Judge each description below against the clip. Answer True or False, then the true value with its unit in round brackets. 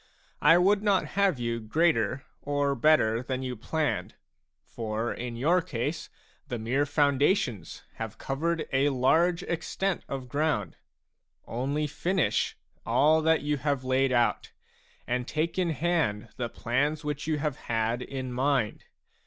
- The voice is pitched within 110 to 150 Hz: True (140 Hz)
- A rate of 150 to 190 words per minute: False (140 wpm)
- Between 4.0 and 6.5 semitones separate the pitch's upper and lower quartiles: True (4.7 semitones)